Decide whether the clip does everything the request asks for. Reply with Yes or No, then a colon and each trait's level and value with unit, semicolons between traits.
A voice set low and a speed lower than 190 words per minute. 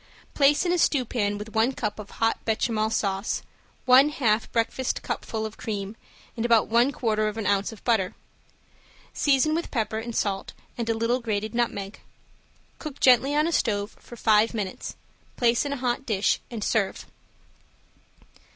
No: high, 225 Hz; average, 165 wpm